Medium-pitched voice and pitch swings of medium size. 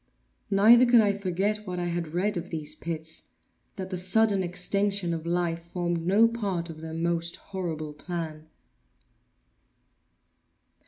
Yes: medium, 175 Hz; average, 3.2 semitones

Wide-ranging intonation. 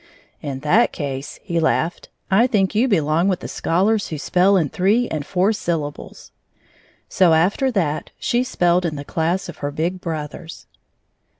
No: average, 4.2 semitones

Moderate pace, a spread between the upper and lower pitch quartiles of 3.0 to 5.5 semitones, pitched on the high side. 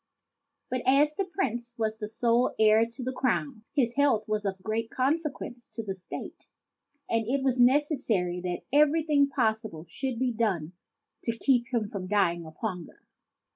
Yes: average, 165 wpm; average, 3.9 semitones; high, 230 Hz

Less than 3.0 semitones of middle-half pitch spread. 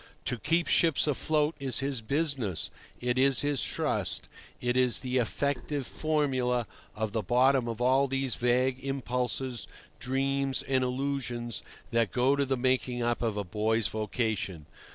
Yes: narrow, 2.5 semitones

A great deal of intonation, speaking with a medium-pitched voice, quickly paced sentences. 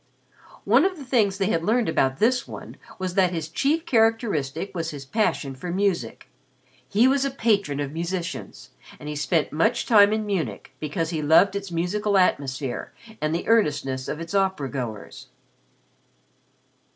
No: wide, 6.1 semitones; medium, 180 Hz; average, 165 wpm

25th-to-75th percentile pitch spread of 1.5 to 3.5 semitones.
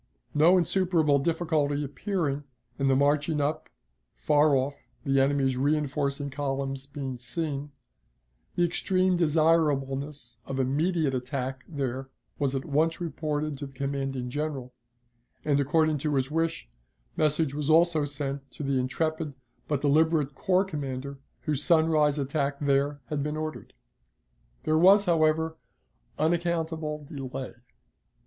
Yes: narrow, 2.5 semitones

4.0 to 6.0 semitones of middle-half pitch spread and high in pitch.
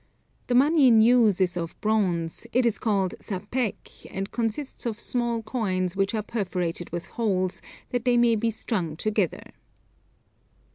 Yes: average, 4.3 semitones; high, 215 Hz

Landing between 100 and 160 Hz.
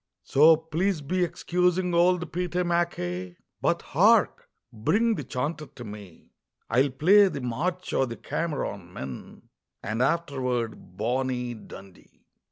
Yes: medium, 140 Hz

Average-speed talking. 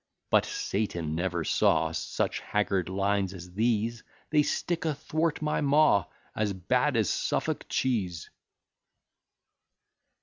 No: slow, 110 wpm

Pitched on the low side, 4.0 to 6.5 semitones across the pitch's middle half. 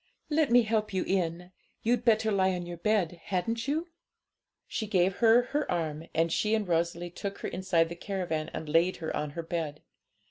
No: medium, 185 Hz; average, 4.6 semitones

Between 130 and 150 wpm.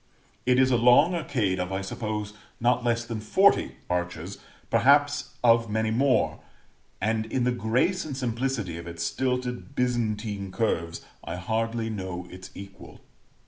Yes: average, 145 wpm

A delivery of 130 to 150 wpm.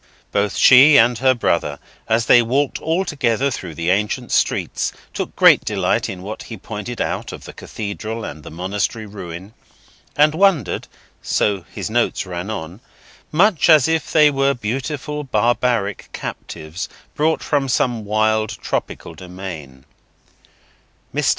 Yes: slow, 135 wpm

